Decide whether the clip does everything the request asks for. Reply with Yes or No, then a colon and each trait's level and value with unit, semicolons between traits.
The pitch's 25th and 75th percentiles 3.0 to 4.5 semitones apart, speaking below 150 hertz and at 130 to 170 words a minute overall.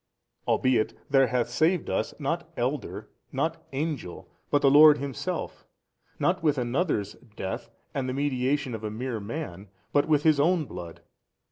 Yes: average, 4.1 semitones; low, 135 Hz; average, 150 wpm